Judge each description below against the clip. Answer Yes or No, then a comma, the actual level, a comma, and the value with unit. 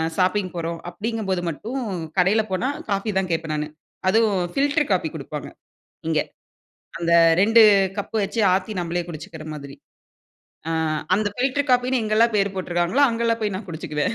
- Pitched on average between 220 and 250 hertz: No, high, 195 Hz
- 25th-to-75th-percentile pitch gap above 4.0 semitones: Yes, average, 4.9 semitones